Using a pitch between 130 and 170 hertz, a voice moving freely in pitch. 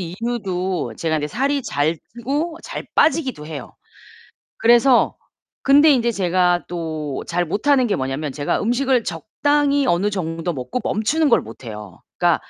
No: high, 195 Hz; wide, 8.6 semitones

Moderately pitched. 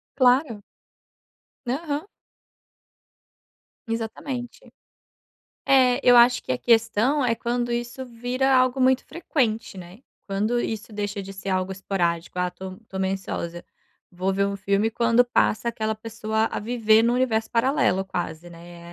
No: high, 225 Hz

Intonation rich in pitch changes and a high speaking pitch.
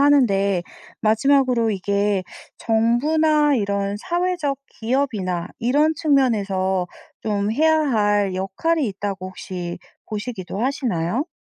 Yes: wide, 6.1 semitones; high, 220 Hz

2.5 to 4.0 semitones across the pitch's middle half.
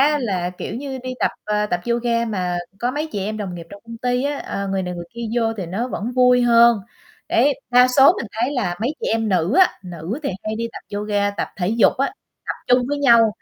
Yes: average, 3.7 semitones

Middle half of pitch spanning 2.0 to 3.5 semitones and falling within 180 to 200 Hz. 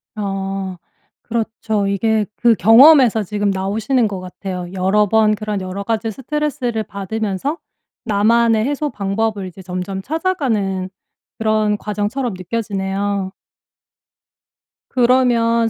No: average, 3.0 semitones; high, 215 Hz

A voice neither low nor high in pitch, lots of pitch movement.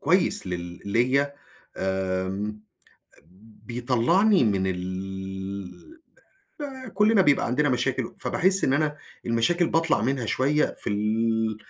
No: low, 120 Hz; wide, 7.7 semitones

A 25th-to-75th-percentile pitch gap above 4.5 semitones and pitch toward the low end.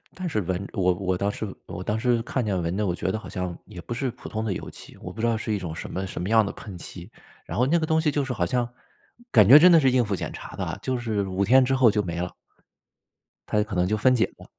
Yes: average, 5.1 semitones; low, 105 Hz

